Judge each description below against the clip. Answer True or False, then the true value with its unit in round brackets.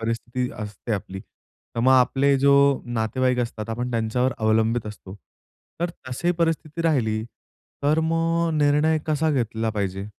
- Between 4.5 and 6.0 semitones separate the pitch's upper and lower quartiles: True (5.1 semitones)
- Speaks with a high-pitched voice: False (125 Hz)